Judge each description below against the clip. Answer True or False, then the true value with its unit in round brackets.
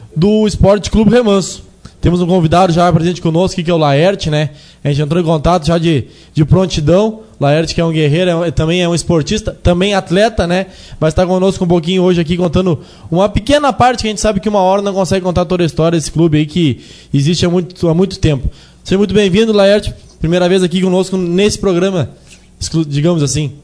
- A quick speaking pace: True (210 wpm)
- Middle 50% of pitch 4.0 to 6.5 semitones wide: False (2.9 semitones)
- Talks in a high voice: False (180 Hz)